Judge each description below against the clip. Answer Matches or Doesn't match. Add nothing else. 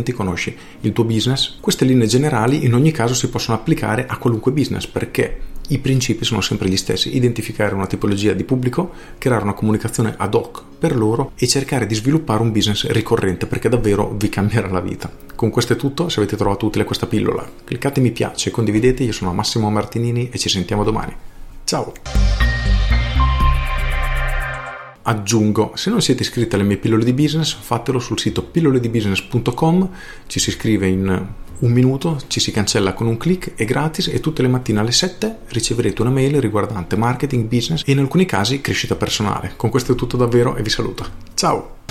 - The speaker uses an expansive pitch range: Doesn't match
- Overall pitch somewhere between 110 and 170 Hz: Matches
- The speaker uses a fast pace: Matches